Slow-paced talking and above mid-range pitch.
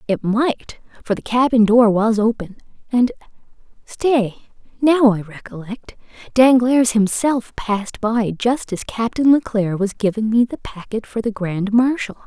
Yes: slow, 130 wpm; high, 225 Hz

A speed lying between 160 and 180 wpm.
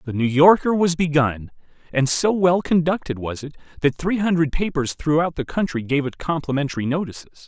Yes: average, 175 wpm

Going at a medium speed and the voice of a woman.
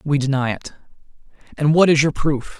No: average, 185 wpm; male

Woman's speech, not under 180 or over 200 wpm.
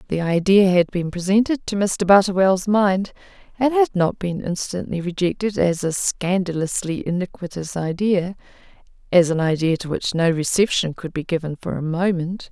No: female; average, 160 wpm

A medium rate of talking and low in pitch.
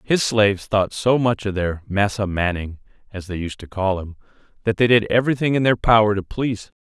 No: fast, 220 wpm; low, 105 Hz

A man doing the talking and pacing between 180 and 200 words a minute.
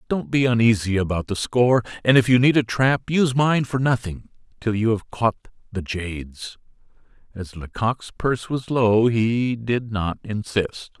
No: male; average, 170 wpm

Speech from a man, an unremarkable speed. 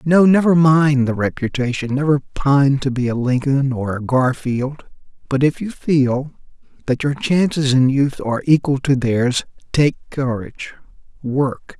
Yes: male; average, 150 wpm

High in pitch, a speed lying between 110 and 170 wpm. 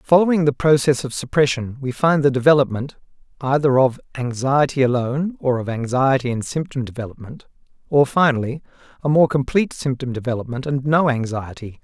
No: low, 135 Hz; average, 145 wpm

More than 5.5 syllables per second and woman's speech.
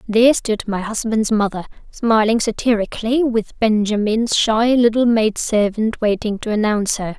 No: 4.8 syllables/s; female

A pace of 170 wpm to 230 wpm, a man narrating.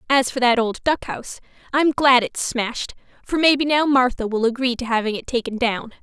No: average, 200 wpm; female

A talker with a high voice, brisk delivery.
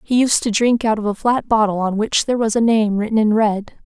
Yes: high, 220 Hz; fast, 280 wpm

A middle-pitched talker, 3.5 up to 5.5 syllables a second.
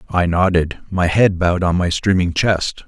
No: very low, 90 Hz; 4.6 syllables/s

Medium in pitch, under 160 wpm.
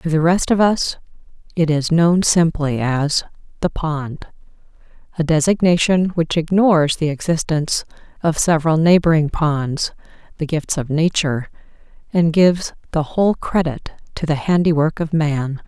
Yes: medium, 160 Hz; slow, 135 wpm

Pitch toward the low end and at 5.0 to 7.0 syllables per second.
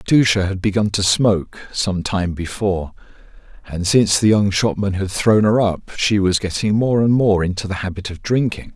Yes: low, 100 Hz; 5.2 syllables/s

